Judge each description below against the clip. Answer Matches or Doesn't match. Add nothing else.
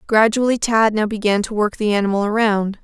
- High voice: Matches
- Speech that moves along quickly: Doesn't match